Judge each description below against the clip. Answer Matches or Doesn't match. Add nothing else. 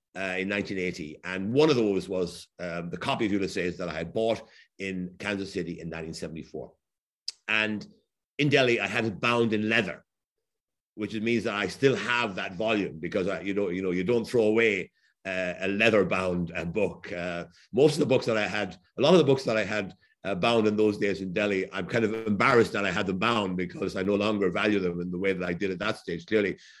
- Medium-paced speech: Doesn't match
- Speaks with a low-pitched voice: Matches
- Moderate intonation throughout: Matches